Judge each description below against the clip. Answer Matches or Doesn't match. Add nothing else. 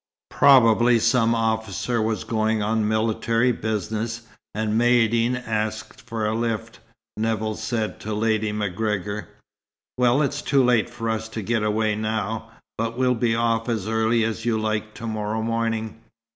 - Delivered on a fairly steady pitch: Matches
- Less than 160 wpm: Matches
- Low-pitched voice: Matches